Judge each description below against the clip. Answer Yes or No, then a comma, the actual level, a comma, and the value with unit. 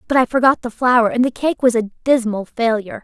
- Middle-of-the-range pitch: No, high, 240 Hz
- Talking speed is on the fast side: Yes, fast, 235 wpm